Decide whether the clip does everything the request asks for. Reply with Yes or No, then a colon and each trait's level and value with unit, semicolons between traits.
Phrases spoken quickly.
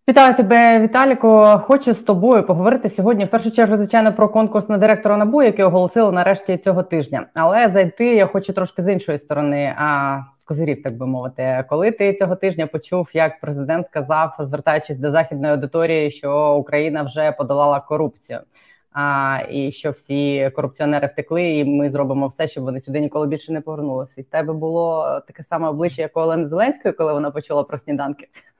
Yes: fast, 175 wpm